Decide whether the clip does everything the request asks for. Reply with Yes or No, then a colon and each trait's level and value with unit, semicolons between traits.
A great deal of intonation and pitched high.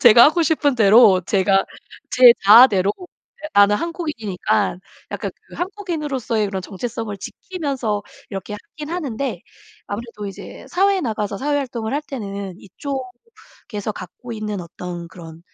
Yes: wide, 6.2 semitones; high, 225 Hz